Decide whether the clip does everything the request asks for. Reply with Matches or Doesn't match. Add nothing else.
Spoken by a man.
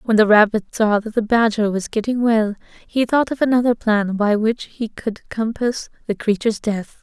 Doesn't match